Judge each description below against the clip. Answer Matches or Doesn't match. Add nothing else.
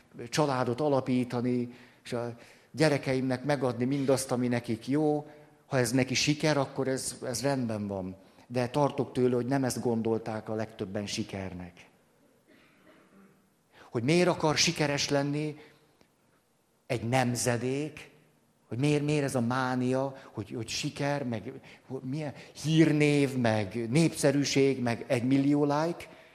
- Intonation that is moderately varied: Matches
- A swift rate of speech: Doesn't match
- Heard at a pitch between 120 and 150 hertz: Matches